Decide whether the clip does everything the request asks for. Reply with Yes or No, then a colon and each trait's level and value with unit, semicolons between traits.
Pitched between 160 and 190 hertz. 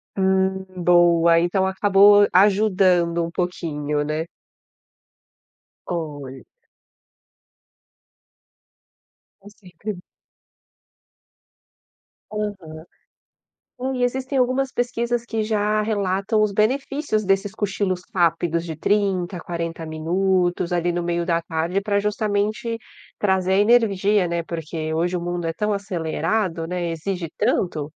Yes: medium, 185 Hz